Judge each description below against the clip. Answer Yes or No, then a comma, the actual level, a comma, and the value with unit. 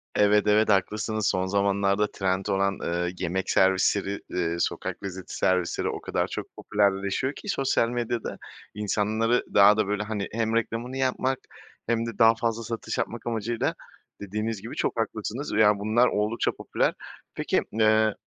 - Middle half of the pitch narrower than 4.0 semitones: Yes, narrow, 2.4 semitones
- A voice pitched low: Yes, low, 105 Hz